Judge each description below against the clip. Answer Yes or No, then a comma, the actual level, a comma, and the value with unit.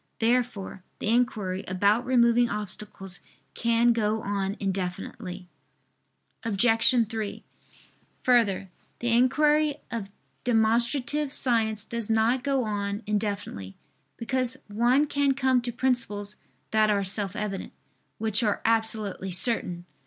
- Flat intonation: No, average, 3.2 semitones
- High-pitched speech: Yes, high, 225 Hz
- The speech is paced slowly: Yes, slow, 110 wpm